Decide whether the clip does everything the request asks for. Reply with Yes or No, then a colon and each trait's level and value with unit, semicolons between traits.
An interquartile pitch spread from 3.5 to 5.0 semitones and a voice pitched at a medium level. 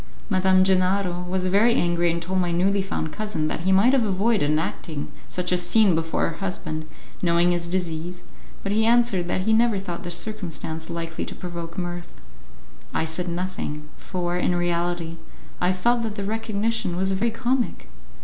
No: average, 2.8 semitones; medium, 180 Hz